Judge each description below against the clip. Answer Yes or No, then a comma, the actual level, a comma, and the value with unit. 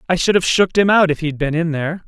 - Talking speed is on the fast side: Yes, fast, 320 wpm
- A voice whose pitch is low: No, medium, 170 Hz